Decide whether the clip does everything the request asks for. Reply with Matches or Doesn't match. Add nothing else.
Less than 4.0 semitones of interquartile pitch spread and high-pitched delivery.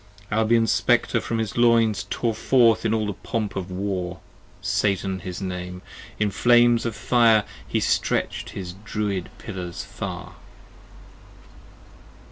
Doesn't match